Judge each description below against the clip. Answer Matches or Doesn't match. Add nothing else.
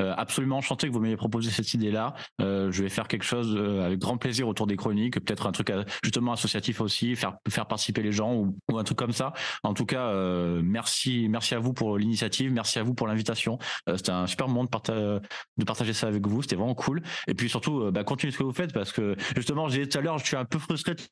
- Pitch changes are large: Doesn't match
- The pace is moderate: Doesn't match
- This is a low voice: Matches